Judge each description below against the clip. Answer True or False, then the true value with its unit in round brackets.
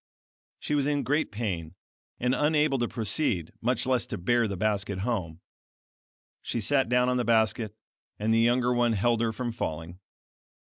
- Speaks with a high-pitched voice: False (115 Hz)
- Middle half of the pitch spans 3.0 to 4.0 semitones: True (3.5 semitones)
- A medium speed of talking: True (165 wpm)